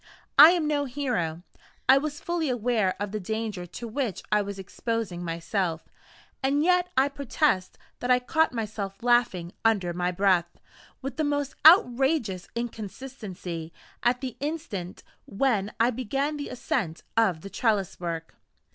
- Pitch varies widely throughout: Yes, wide, 6.5 semitones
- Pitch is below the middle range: No, high, 230 Hz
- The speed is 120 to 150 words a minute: Yes, average, 145 wpm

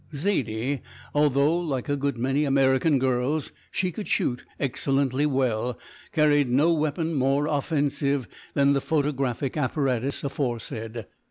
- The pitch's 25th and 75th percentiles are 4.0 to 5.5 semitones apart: No, narrow, 2.4 semitones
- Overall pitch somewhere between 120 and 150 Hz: Yes, medium, 140 Hz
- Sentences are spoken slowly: Yes, slow, 120 wpm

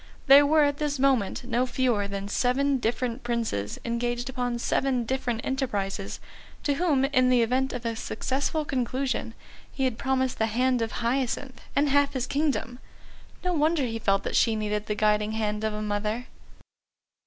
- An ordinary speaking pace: Yes, average, 170 wpm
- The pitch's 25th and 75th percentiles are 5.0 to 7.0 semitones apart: No, average, 3.4 semitones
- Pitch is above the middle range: Yes, high, 245 Hz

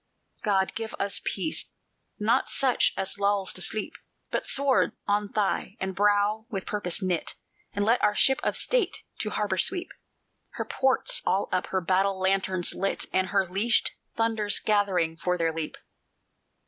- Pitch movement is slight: Yes, narrow, 2.3 semitones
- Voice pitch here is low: No, high, 200 Hz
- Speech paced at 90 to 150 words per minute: No, average, 160 wpm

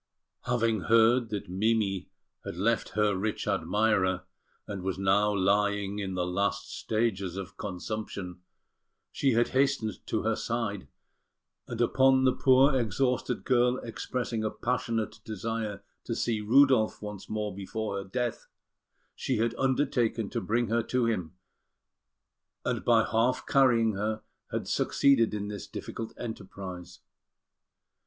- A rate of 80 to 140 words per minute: Yes, slow, 135 wpm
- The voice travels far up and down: No, average, 3.1 semitones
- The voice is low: Yes, low, 110 Hz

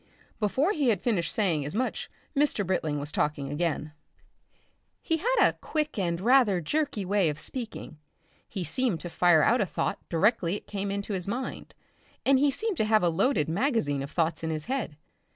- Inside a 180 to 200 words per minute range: Yes, average, 190 wpm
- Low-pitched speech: No, high, 200 Hz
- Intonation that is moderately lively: No, wide, 7.7 semitones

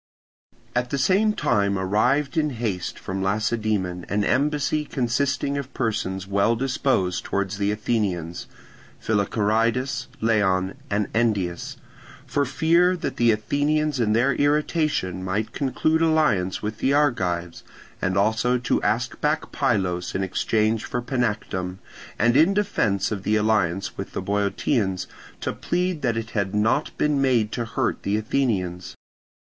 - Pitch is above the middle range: No, low, 110 Hz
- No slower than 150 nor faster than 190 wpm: No, slow, 135 wpm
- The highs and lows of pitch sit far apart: Yes, wide, 5.8 semitones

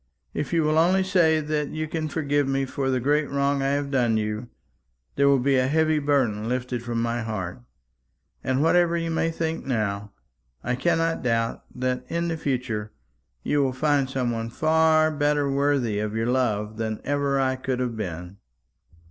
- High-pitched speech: No, low, 135 Hz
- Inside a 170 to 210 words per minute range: Yes, average, 180 wpm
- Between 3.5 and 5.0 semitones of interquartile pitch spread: Yes, average, 4.5 semitones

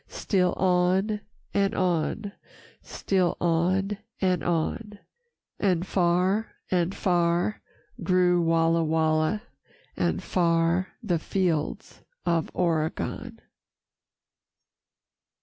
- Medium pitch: Yes, medium, 180 Hz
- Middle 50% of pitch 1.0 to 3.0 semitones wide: Yes, narrow, 2.4 semitones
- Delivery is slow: Yes, slow, 80 wpm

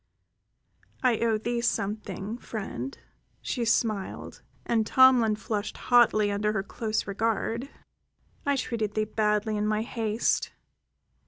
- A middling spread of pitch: No, narrow, 1.8 semitones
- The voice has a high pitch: Yes, high, 220 Hz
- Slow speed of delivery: Yes, slow, 115 wpm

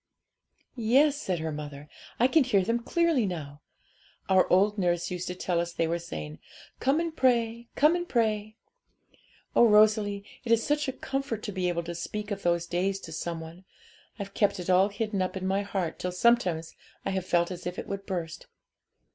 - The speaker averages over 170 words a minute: Yes, average, 195 wpm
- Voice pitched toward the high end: Yes, high, 195 Hz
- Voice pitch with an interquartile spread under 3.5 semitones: No, average, 5.0 semitones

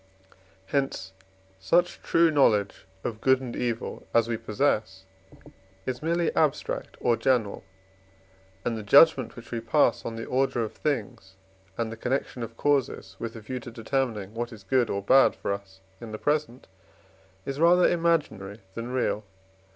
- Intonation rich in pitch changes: No, average, 3.9 semitones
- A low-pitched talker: Yes, low, 120 Hz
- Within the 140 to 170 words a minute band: Yes, average, 160 wpm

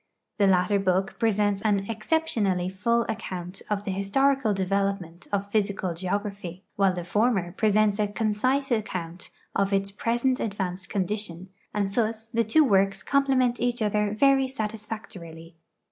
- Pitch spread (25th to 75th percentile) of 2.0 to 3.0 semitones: Yes, average, 2.7 semitones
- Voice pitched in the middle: No, high, 205 Hz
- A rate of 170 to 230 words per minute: No, average, 140 wpm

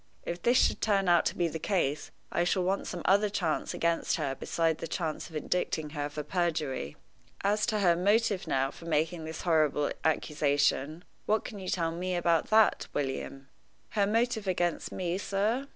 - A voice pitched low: No, medium, 170 Hz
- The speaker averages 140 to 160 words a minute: No, average, 185 wpm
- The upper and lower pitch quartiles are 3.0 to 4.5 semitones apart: Yes, average, 4.2 semitones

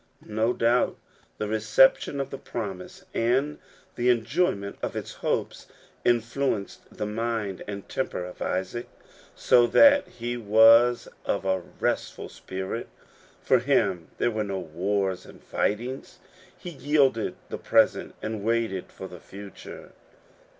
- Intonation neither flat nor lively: Yes, average, 3.5 semitones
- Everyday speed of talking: No, slow, 130 wpm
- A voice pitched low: Yes, low, 115 Hz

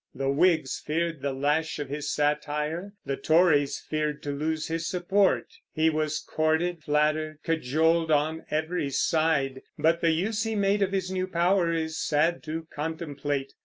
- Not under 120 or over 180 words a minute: Yes, average, 160 wpm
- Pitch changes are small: Yes, narrow, 2.3 semitones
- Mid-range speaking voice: Yes, medium, 160 Hz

